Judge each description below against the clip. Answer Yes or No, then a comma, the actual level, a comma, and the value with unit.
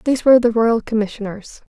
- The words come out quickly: No, average, 170 wpm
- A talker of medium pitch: No, high, 225 Hz